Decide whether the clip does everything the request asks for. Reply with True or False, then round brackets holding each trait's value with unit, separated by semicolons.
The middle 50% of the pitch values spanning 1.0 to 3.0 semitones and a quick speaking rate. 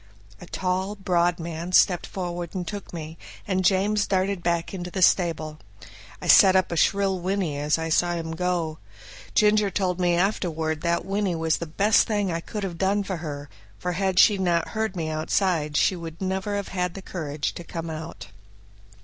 False (2.7 semitones; 185 wpm)